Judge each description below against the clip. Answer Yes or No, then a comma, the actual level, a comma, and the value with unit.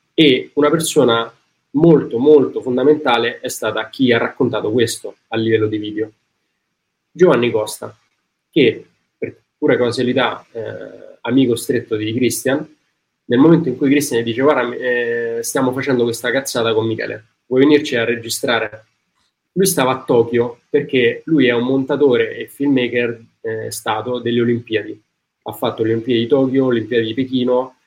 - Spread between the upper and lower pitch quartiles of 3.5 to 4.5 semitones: No, narrow, 2.6 semitones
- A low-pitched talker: Yes, low, 120 Hz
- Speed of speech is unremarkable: Yes, average, 150 wpm